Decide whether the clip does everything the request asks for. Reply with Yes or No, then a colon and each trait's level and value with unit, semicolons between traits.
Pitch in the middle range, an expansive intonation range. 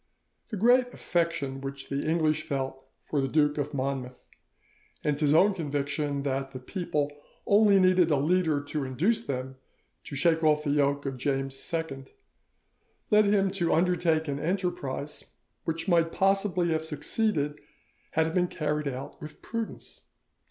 No: medium, 150 Hz; average, 4.2 semitones